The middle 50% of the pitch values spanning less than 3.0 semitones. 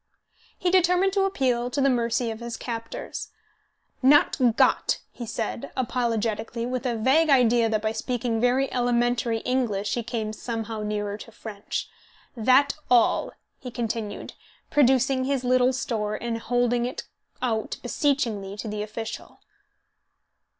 Yes: narrow, 2.5 semitones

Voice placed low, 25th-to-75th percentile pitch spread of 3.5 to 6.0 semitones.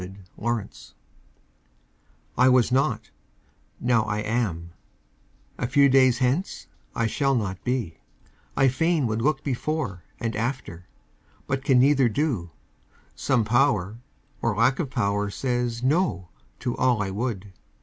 Yes: low, 120 Hz; average, 4.1 semitones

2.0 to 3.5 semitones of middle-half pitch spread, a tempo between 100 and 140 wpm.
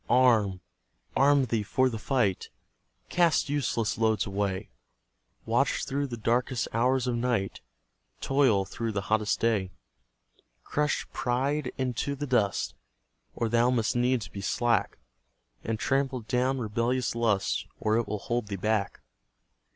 Yes: average, 3.1 semitones; slow, 135 wpm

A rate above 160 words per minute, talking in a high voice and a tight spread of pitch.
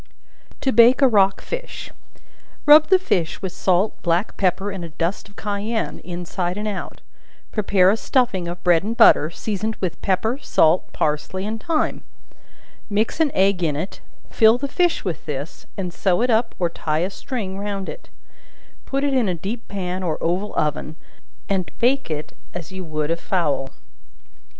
No: average, 175 wpm; high, 195 Hz; average, 4.3 semitones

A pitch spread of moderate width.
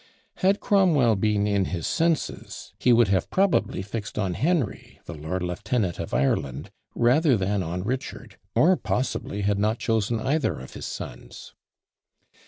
No: wide, 6.1 semitones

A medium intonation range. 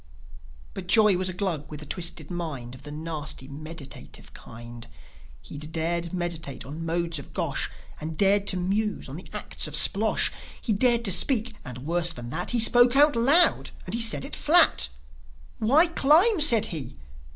No: wide, 7.1 semitones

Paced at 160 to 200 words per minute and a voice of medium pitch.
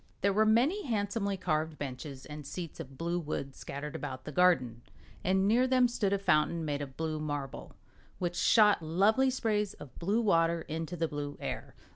Yes: average, 180 wpm; medium, 170 Hz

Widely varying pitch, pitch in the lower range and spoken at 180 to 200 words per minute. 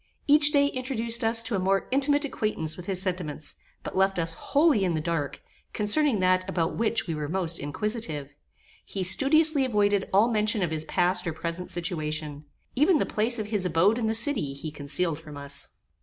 No: wide, 6.0 semitones; high, 190 Hz; average, 190 wpm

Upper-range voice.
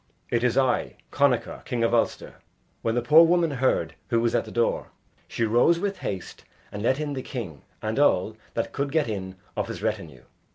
No: low, 120 Hz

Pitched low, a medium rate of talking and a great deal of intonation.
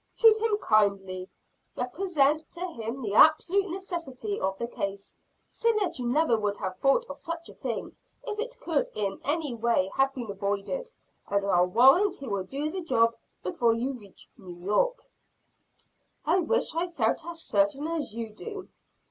No: very high, 275 Hz; average, 170 wpm; wide, 8.6 semitones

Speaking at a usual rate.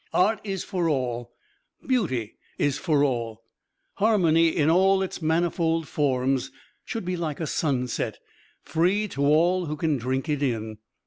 Yes: average, 150 wpm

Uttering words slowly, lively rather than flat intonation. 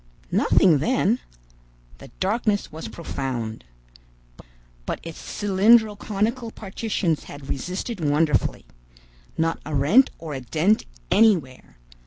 Yes: slow, 105 wpm; wide, 6.8 semitones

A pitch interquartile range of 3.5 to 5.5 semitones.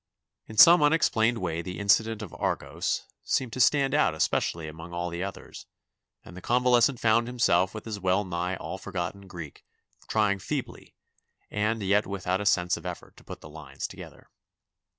Yes: average, 4.3 semitones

